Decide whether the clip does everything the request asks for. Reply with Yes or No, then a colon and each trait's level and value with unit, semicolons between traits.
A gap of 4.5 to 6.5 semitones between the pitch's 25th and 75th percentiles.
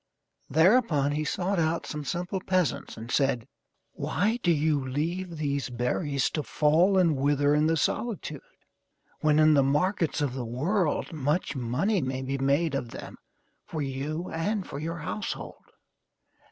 No: average, 4.1 semitones